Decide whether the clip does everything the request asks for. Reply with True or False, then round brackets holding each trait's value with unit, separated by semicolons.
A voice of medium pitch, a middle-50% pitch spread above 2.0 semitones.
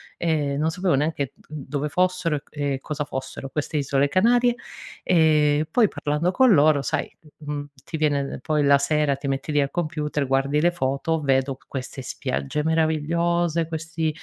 True (150 Hz; 2.6 semitones)